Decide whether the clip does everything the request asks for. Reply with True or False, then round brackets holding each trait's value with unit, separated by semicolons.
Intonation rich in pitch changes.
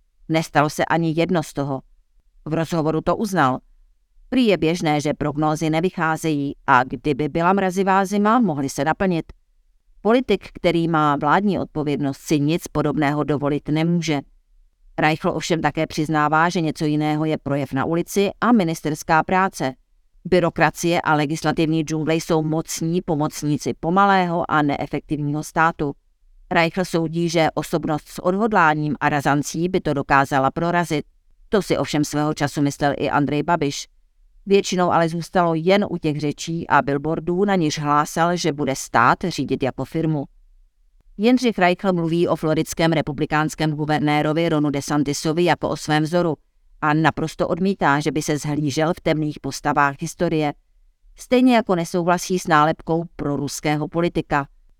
False (2.7 semitones)